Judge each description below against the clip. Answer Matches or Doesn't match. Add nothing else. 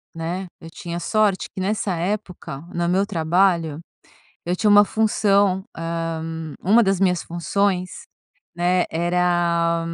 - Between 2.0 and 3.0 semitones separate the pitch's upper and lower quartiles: Matches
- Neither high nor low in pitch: Matches